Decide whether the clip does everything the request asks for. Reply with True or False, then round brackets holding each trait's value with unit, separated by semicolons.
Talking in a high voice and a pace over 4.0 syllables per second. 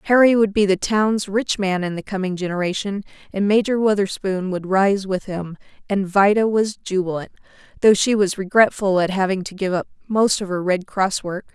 True (195 Hz; 5.1 syllables/s)